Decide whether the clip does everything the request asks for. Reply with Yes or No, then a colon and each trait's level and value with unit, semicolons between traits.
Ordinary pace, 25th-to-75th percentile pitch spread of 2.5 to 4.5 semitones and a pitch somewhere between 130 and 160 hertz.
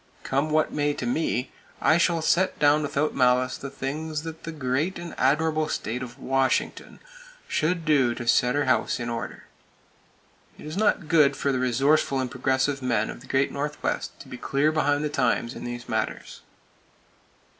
Yes: average, 175 wpm; average, 3.4 semitones; medium, 140 Hz